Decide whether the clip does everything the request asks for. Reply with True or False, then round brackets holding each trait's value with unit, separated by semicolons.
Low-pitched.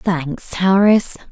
False (185 Hz)